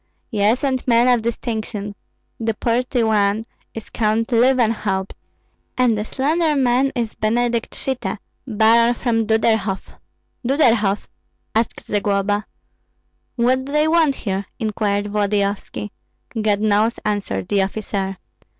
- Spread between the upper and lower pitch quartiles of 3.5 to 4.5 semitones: No, average, 2.8 semitones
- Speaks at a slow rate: Yes, slow, 115 wpm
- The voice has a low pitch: No, high, 225 Hz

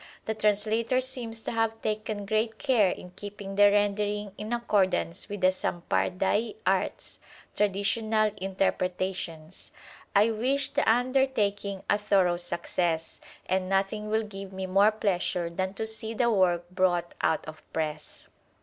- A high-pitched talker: Yes, high, 205 Hz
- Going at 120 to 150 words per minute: Yes, average, 145 wpm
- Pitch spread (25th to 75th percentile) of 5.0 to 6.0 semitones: No, average, 2.9 semitones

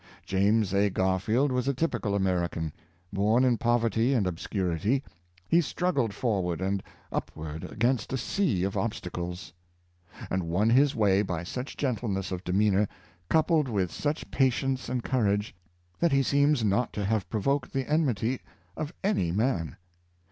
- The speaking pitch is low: Yes, low, 110 Hz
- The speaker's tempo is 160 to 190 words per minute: No, average, 150 wpm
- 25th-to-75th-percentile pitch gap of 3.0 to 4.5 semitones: No, wide, 5.6 semitones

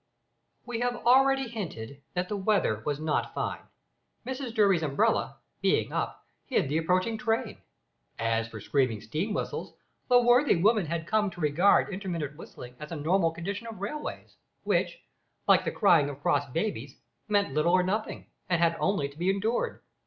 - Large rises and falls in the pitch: Yes, wide, 6.5 semitones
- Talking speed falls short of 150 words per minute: No, average, 165 wpm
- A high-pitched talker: No, medium, 180 Hz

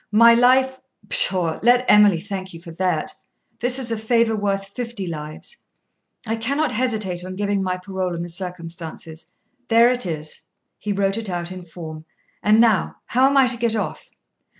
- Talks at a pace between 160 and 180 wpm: Yes, average, 175 wpm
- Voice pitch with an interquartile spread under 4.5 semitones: No, average, 4.9 semitones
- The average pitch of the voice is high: Yes, high, 200 Hz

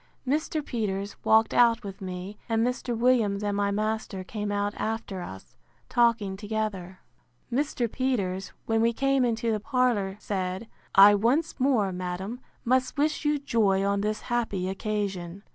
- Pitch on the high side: Yes, high, 215 Hz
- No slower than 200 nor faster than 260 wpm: No, average, 150 wpm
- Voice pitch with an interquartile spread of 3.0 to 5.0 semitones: Yes, average, 3.5 semitones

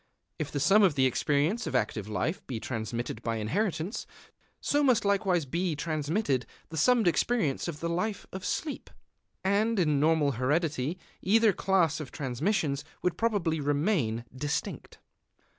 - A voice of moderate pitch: Yes, medium, 160 Hz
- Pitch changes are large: Yes, wide, 6.0 semitones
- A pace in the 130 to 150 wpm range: Yes, average, 145 wpm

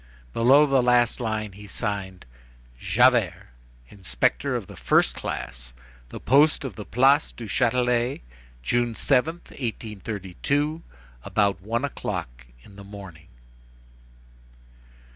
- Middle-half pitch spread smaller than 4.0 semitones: No, average, 4.4 semitones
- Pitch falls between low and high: No, low, 115 Hz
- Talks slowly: Yes, slow, 110 wpm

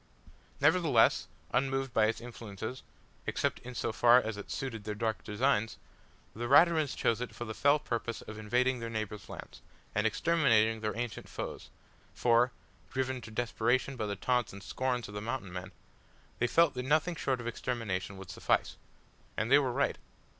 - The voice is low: Yes, low, 120 Hz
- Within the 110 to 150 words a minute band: No, average, 175 wpm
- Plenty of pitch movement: No, average, 3.2 semitones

